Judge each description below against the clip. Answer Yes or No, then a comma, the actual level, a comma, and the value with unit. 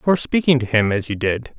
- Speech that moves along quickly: Yes, fast, 265 wpm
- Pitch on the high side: No, low, 125 Hz